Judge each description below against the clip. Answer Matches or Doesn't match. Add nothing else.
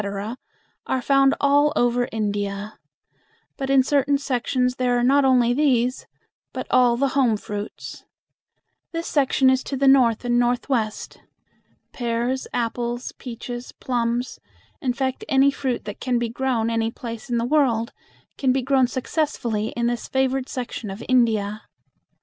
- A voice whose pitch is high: Matches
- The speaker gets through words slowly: Doesn't match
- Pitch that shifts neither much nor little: Doesn't match